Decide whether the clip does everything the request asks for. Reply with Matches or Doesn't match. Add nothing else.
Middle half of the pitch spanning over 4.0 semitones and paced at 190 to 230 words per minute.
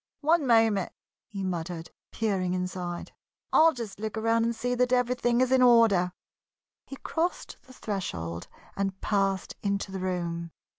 Doesn't match